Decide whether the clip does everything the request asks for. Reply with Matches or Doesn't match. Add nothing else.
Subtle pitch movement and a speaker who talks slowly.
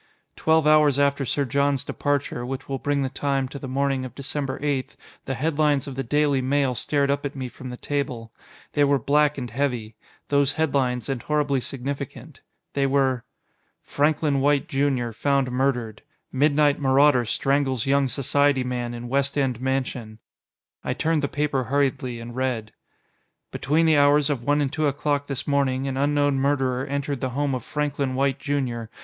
Doesn't match